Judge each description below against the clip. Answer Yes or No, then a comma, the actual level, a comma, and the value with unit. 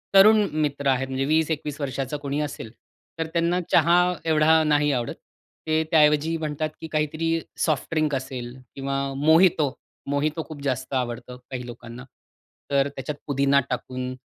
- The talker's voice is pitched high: No, medium, 145 Hz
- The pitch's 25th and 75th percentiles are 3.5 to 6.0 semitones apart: No, average, 2.9 semitones